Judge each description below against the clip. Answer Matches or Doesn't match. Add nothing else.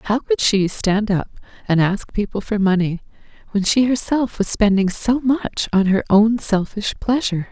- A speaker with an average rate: Matches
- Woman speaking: Matches